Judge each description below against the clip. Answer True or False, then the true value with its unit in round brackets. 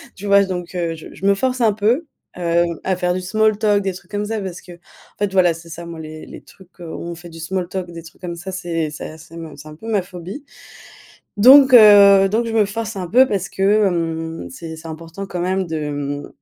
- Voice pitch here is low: False (180 Hz)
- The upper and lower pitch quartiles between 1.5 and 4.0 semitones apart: True (3.5 semitones)